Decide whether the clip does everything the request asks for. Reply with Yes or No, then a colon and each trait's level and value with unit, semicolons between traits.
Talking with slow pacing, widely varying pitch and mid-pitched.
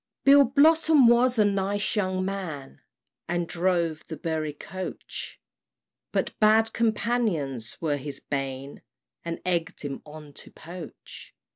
Yes: slow, 125 wpm; wide, 6.5 semitones; medium, 180 Hz